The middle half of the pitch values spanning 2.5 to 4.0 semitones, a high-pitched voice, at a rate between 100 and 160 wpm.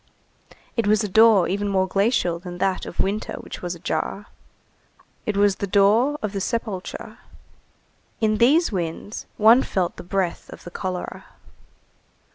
Yes: average, 2.8 semitones; high, 200 Hz; average, 150 wpm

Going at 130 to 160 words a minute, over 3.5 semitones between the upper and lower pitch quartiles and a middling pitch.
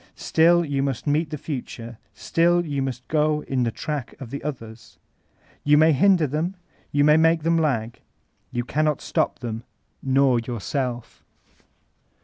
Yes: average, 150 wpm; average, 4.1 semitones; medium, 145 Hz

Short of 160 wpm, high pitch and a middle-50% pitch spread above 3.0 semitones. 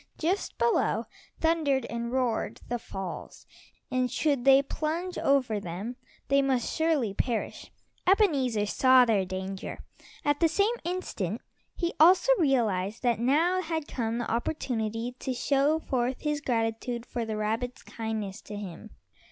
Yes: average, 140 wpm; very high, 250 Hz; average, 5.1 semitones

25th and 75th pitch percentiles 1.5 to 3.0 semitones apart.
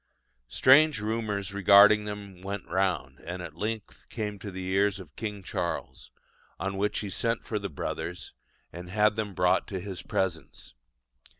Yes: narrow, 2.4 semitones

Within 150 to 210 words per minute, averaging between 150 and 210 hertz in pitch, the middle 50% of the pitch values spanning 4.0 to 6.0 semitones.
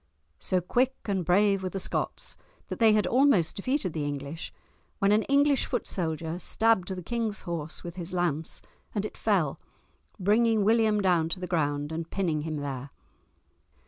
Yes: average, 170 wpm; medium, 185 Hz; average, 5.0 semitones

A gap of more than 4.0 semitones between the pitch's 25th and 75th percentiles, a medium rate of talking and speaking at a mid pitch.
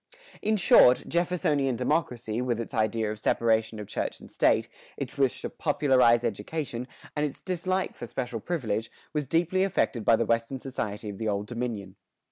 No: average, 4.9 semitones; average, 170 wpm; low, 120 Hz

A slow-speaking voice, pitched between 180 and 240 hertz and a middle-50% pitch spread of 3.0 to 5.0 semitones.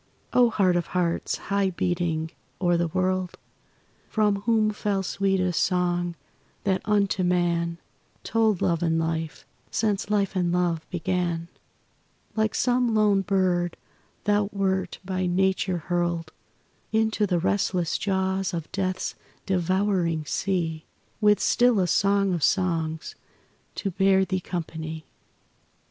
No: slow, 125 wpm; medium, 185 Hz; narrow, 2.5 semitones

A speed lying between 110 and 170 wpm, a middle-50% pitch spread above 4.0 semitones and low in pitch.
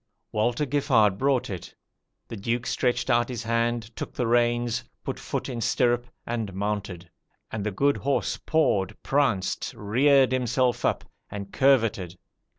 No: average, 145 wpm; average, 3.4 semitones; low, 120 Hz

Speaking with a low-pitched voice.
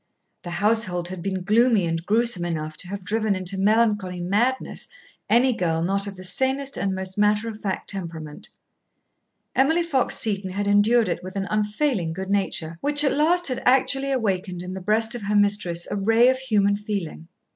No: high, 205 Hz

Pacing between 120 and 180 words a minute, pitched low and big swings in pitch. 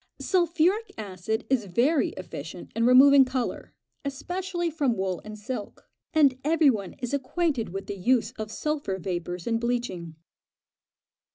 No: average, 140 wpm; high, 245 Hz; wide, 6.5 semitones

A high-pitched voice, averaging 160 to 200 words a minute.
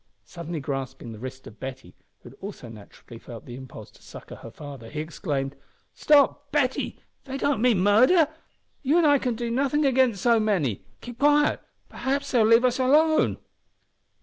Yes: high, 220 Hz; average, 175 wpm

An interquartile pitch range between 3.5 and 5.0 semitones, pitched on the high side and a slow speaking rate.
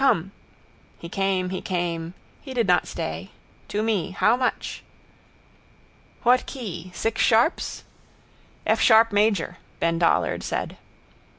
Yes: average, 4.5 semitones; high, 195 Hz; slow, 120 wpm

